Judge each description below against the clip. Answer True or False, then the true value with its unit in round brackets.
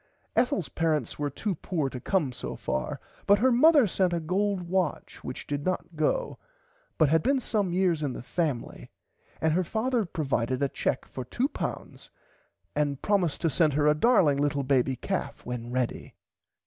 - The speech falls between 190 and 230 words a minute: False (175 wpm)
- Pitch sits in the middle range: True (160 Hz)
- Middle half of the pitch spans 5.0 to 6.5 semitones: True (5.6 semitones)